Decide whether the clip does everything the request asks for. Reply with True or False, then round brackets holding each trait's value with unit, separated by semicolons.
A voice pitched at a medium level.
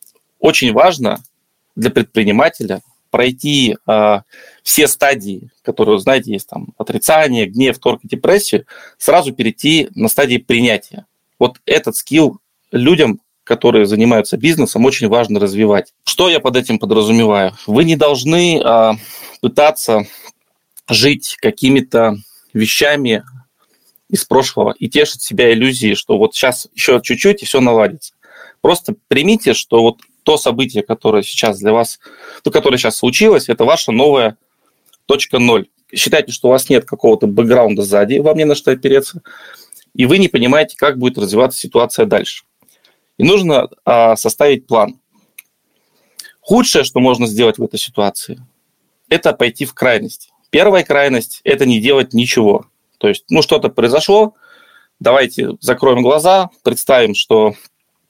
False (125 Hz)